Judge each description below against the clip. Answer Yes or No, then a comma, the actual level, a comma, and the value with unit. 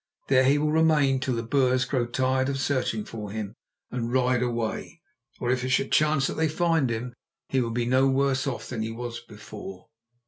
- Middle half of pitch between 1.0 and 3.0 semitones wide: Yes, narrow, 2.5 semitones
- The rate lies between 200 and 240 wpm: Yes, fast, 205 wpm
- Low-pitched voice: Yes, low, 130 Hz